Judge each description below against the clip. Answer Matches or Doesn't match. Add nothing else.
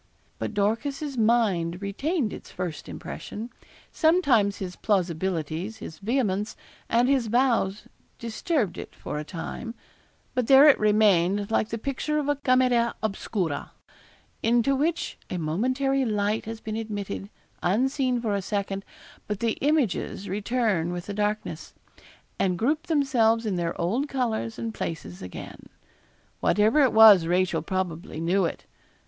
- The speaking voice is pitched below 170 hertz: Doesn't match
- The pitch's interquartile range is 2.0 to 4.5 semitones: Doesn't match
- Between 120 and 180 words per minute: Matches